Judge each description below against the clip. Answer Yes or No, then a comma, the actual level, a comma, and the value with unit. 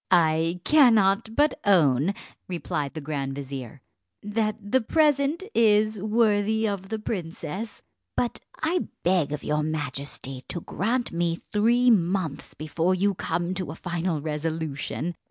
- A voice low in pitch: No, medium, 185 Hz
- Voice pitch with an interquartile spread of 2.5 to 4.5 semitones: No, wide, 5.6 semitones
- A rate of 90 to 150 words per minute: Yes, slow, 135 wpm